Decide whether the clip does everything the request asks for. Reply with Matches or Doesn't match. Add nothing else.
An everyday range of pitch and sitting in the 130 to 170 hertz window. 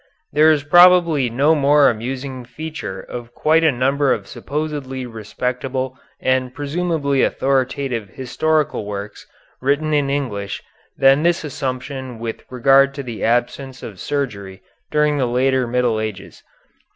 Matches